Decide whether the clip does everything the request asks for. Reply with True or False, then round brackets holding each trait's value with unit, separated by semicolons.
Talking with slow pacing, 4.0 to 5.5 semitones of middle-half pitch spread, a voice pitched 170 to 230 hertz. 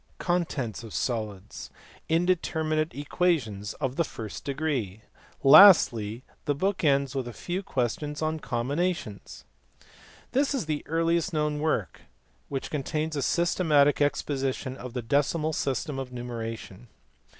False (130 wpm; 4.7 semitones; 145 Hz)